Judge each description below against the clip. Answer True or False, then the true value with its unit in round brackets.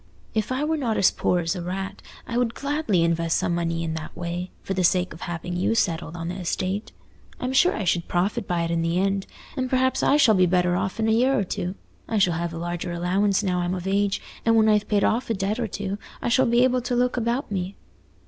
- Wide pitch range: False (4.6 semitones)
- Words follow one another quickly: True (255 wpm)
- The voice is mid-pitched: False (195 Hz)